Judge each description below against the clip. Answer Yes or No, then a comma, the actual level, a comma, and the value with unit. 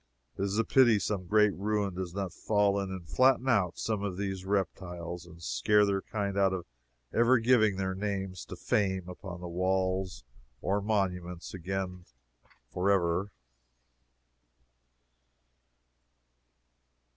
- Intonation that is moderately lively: No, narrow, 2.0 semitones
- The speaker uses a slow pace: Yes, slow, 130 wpm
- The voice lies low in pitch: Yes, very low, 95 Hz